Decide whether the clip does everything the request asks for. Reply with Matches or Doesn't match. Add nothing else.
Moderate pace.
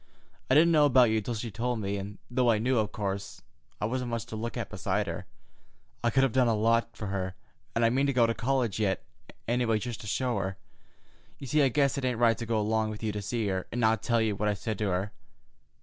Doesn't match